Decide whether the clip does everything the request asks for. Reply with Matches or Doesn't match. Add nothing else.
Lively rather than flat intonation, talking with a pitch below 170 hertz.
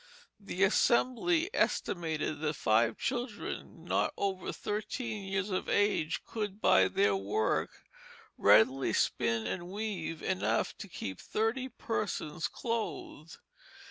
Doesn't match